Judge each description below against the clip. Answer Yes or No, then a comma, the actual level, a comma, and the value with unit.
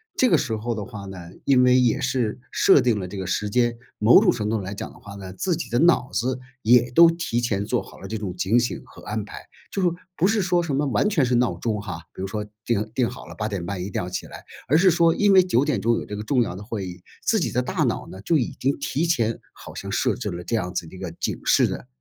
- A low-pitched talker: Yes, low, 115 Hz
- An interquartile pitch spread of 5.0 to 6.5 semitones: Yes, wide, 5.5 semitones